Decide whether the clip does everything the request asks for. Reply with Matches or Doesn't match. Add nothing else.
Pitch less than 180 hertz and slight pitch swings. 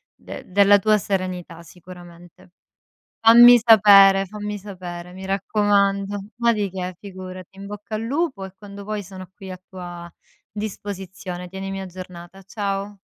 Doesn't match